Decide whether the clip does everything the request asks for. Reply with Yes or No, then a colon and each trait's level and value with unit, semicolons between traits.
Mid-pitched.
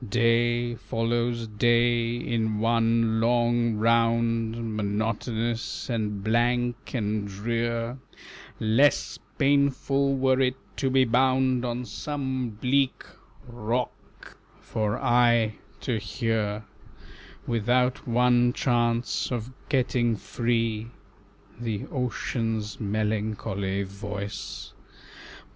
No: low, 115 Hz